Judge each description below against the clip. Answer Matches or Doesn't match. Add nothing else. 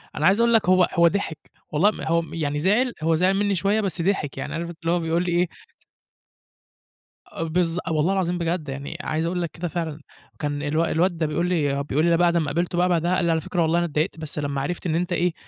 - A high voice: Doesn't match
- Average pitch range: Doesn't match